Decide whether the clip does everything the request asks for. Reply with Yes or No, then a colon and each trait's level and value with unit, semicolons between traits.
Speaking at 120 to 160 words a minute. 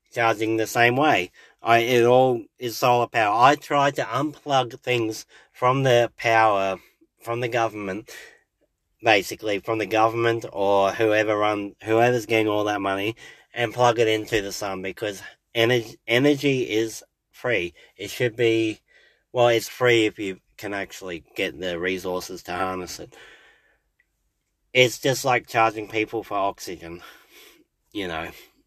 Yes: average, 145 wpm